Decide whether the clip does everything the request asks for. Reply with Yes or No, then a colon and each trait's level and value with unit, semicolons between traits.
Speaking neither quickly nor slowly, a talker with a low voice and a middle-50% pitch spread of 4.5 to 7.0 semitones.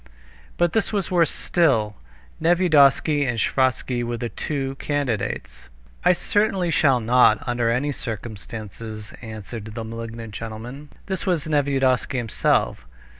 No: slow, 125 wpm; low, 125 Hz; average, 4.9 semitones